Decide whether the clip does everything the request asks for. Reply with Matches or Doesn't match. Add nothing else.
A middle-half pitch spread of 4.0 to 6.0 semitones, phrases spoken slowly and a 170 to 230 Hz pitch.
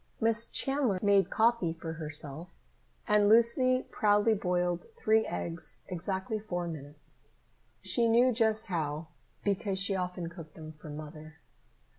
Matches